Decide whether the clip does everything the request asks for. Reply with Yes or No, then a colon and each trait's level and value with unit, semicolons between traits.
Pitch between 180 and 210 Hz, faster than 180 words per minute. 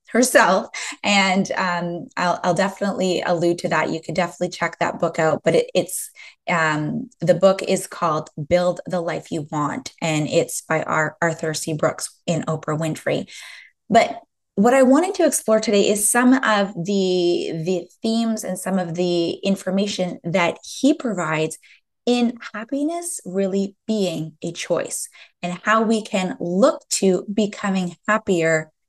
No: medium, 185 Hz; average, 155 wpm